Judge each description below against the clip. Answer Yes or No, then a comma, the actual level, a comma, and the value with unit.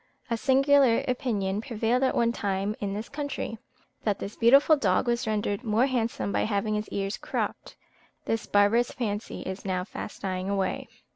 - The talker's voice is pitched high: Yes, high, 215 Hz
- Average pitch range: Yes, average, 3.3 semitones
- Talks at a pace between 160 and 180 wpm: Yes, average, 165 wpm